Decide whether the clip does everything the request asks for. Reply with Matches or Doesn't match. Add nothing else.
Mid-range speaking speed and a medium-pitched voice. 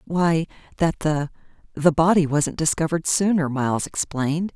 Doesn't match